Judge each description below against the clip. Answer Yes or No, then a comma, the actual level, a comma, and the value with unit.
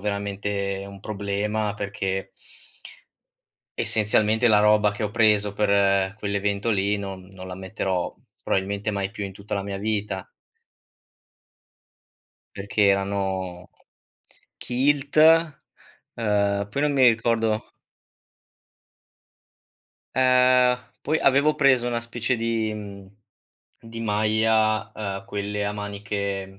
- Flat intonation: Yes, narrow, 2.1 semitones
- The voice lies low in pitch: Yes, low, 105 Hz